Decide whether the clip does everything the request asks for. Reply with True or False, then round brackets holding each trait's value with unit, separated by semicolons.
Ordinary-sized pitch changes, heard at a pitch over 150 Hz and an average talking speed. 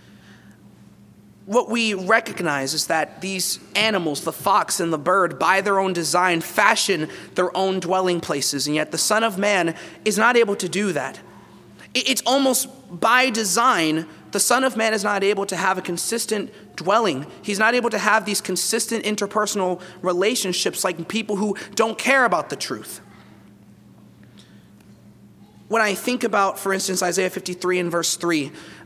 True (4.1 semitones; 190 Hz; 160 wpm)